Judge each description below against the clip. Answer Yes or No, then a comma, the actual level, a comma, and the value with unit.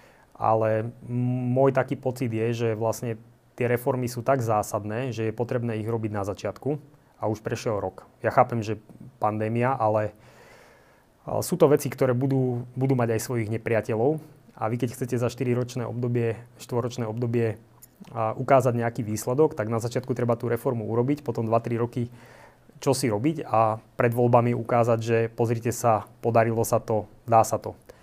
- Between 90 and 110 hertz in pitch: No, low, 120 Hz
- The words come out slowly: No, fast, 165 wpm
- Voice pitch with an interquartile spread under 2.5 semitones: Yes, narrow, 2.1 semitones